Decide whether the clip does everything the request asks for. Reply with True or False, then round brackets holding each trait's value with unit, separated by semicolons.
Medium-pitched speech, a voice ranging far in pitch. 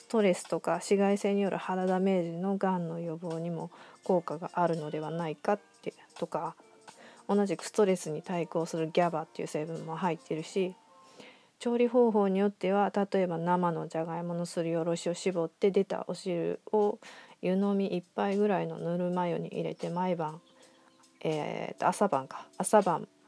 False (180 Hz; 3.1 semitones)